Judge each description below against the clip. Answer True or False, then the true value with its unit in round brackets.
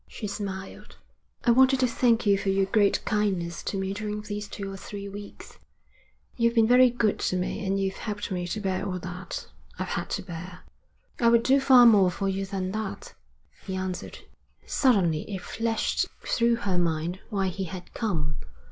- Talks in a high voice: True (200 Hz)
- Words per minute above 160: True (185 wpm)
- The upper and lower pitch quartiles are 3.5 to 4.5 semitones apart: False (3.0 semitones)